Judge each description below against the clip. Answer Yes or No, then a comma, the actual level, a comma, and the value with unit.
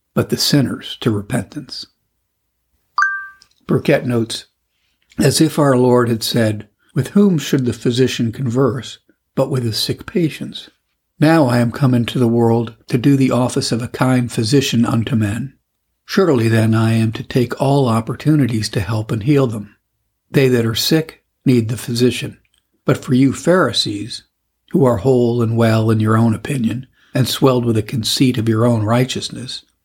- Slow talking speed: No, average, 165 wpm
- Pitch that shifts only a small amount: No, average, 3.2 semitones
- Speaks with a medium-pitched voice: No, low, 120 Hz